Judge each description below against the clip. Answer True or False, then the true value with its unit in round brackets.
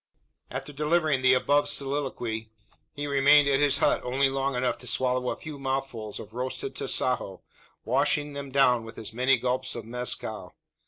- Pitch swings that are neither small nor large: False (2.3 semitones)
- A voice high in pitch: False (135 Hz)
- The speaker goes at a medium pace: True (165 wpm)